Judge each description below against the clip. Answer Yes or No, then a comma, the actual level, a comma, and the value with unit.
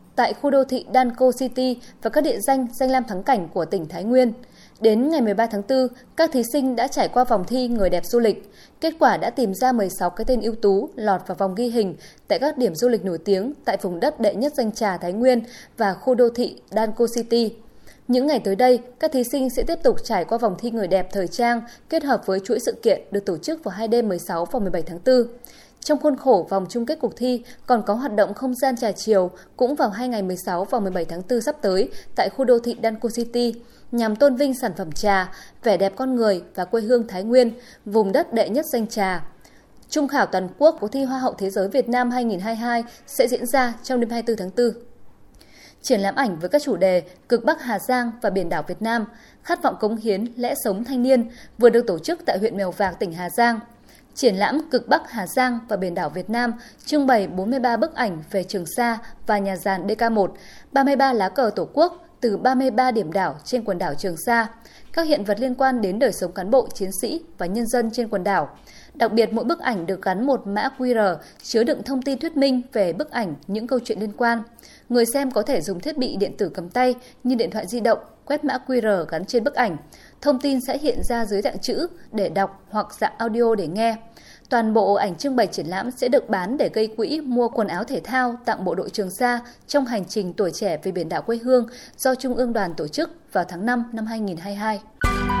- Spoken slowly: No, average, 240 wpm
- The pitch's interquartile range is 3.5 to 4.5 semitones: Yes, average, 4.1 semitones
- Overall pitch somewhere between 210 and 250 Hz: Yes, high, 235 Hz